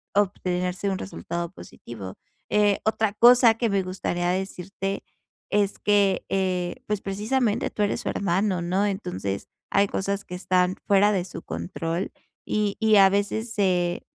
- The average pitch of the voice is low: No, high, 195 Hz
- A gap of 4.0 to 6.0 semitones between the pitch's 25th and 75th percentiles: No, narrow, 2.4 semitones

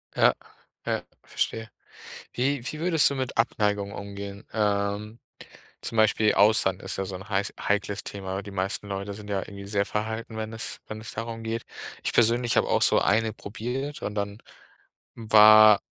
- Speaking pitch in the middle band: No, low, 105 Hz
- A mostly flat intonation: Yes, narrow, 2.0 semitones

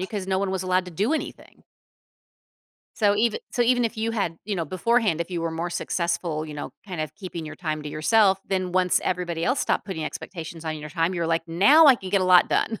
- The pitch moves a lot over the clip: No, average, 3.7 semitones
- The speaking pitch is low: No, medium, 185 Hz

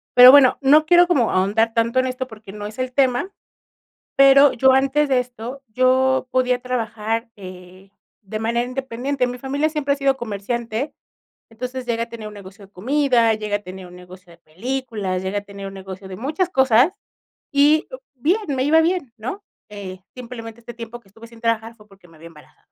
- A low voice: No, high, 235 Hz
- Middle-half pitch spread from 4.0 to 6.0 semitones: Yes, average, 4.3 semitones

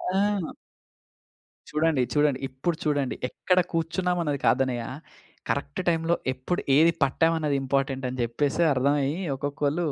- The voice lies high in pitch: No, medium, 145 Hz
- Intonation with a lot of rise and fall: No, average, 3.7 semitones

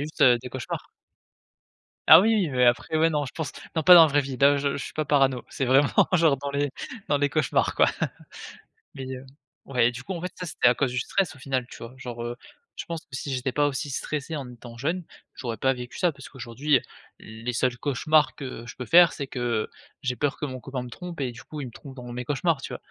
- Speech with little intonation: No, average, 3.3 semitones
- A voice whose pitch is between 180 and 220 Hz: No, low, 135 Hz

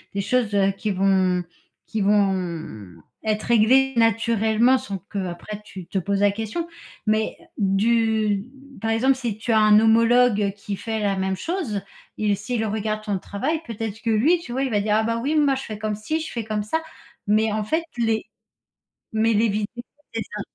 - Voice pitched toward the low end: No, high, 215 Hz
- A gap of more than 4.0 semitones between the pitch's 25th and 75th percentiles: No, narrow, 2.4 semitones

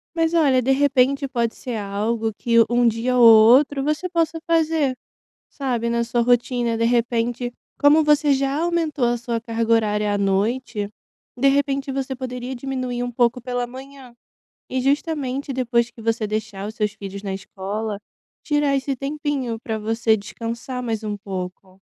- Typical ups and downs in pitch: Yes, average, 3.3 semitones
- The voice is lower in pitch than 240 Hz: No, high, 245 Hz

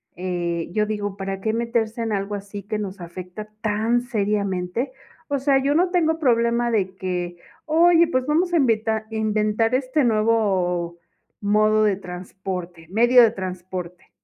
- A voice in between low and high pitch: No, high, 215 Hz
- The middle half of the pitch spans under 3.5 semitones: No, average, 4.2 semitones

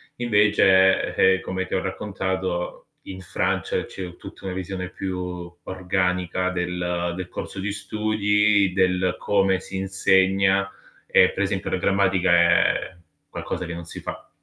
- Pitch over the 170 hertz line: No, very low, 95 Hz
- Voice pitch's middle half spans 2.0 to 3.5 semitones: No, narrow, 1.2 semitones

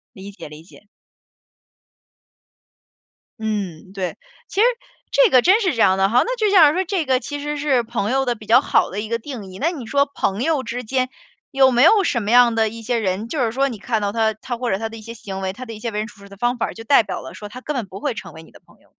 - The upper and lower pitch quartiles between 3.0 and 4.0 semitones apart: No, average, 4.5 semitones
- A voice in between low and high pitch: No, high, 235 Hz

